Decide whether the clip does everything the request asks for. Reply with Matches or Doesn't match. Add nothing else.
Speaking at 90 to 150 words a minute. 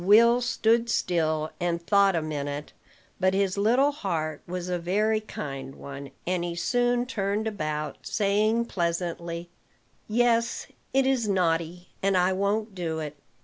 Matches